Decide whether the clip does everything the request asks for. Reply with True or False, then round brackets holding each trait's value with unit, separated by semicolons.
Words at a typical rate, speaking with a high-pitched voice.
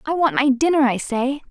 False (240 wpm; 270 Hz)